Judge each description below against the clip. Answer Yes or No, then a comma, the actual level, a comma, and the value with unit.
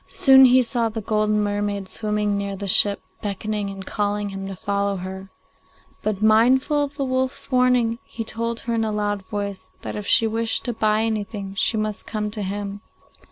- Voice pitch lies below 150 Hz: No, high, 210 Hz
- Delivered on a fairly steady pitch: Yes, narrow, 2.2 semitones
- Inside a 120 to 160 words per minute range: No, average, 195 wpm